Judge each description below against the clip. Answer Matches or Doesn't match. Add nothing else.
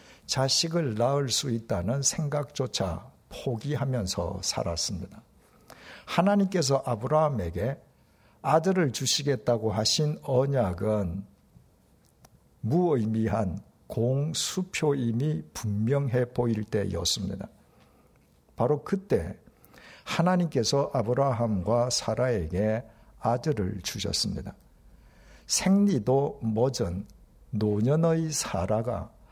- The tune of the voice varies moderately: Matches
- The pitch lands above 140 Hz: Doesn't match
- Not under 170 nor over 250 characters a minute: Matches